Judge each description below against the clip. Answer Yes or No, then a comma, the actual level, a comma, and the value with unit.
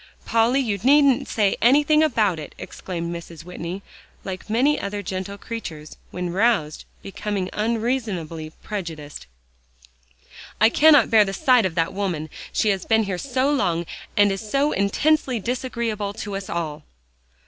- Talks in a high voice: Yes, high, 205 Hz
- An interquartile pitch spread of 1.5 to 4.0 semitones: No, average, 4.9 semitones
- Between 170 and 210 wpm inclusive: No, average, 145 wpm